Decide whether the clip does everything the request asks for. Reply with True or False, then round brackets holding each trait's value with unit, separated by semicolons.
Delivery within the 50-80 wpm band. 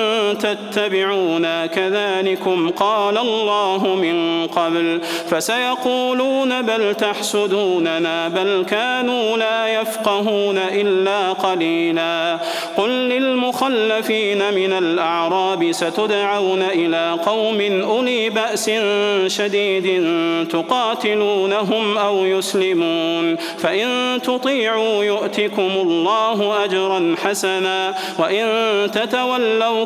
True (70 wpm)